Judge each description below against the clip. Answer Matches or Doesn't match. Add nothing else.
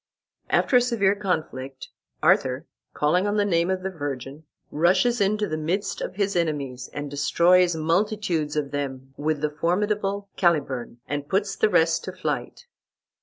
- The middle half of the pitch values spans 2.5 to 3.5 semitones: Doesn't match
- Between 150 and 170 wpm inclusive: Matches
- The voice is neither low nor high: Matches